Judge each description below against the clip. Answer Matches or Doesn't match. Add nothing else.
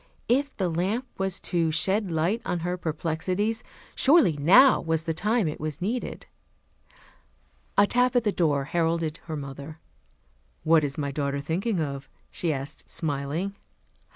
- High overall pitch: Doesn't match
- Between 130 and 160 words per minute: Matches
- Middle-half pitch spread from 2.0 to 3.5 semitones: Doesn't match